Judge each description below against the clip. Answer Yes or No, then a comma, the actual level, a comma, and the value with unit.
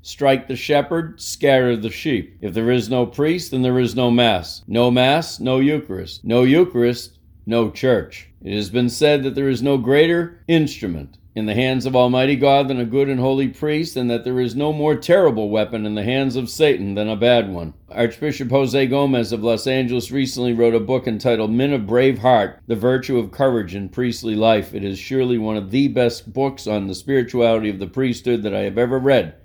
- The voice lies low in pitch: Yes, low, 125 Hz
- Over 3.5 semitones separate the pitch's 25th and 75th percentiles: No, average, 3.2 semitones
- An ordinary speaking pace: No, fast, 210 wpm